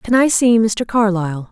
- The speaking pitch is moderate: No, high, 215 Hz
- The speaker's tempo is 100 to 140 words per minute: No, average, 200 wpm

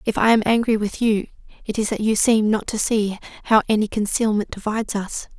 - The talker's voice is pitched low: No, high, 215 Hz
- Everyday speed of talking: No, fast, 210 wpm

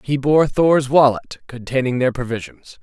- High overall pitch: No, low, 135 Hz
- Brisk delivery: No, average, 150 wpm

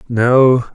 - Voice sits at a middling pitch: No, low, 125 Hz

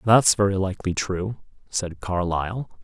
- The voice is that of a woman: No, male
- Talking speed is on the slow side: Yes, slow, 125 wpm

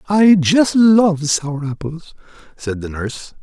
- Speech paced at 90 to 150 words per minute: Yes, average, 140 wpm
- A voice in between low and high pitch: Yes, medium, 165 Hz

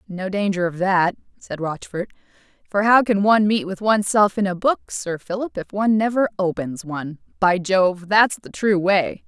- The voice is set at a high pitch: Yes, high, 195 Hz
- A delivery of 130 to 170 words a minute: No, average, 180 wpm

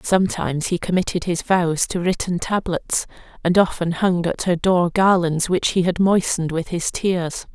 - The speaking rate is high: No, average, 175 wpm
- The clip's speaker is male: No, female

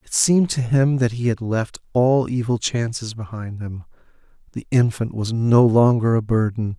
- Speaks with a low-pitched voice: Yes, low, 115 Hz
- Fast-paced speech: No, average, 175 wpm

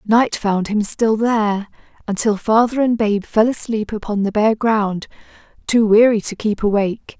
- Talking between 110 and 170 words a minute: Yes, average, 165 wpm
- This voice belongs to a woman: Yes, female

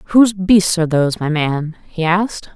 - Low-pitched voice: No, medium, 175 Hz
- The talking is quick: No, average, 190 wpm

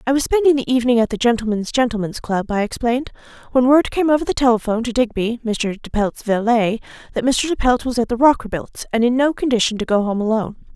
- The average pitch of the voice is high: Yes, high, 240 Hz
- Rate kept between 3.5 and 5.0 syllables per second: No, 6.3 syllables/s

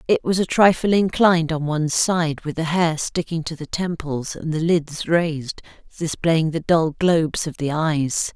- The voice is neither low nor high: Yes, medium, 160 Hz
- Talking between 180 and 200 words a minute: Yes, average, 185 wpm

